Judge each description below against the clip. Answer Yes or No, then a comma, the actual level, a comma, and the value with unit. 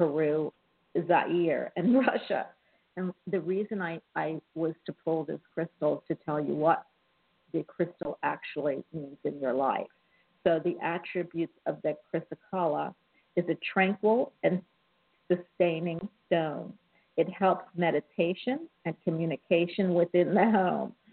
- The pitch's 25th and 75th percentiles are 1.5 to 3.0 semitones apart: Yes, narrow, 2.5 semitones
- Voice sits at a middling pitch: Yes, medium, 175 Hz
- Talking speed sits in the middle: No, slow, 130 wpm